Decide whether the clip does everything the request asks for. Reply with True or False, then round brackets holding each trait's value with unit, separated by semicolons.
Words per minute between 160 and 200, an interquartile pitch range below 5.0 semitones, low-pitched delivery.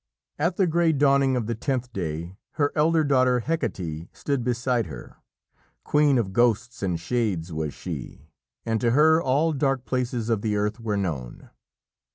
False (165 wpm; 5.4 semitones; 120 Hz)